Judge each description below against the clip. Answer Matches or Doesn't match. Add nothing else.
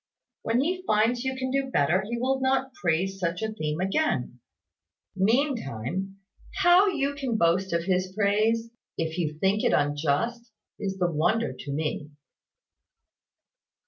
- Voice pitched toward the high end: Matches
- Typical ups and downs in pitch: Doesn't match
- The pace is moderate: Matches